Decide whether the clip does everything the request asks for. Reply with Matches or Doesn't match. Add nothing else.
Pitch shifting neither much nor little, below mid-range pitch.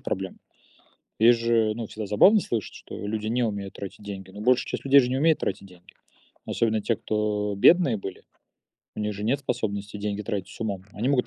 Matches